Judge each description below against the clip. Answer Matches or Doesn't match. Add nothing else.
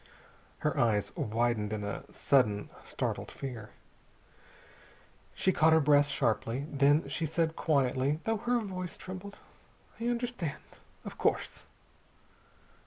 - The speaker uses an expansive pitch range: Matches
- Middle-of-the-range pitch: Matches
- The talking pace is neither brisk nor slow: Doesn't match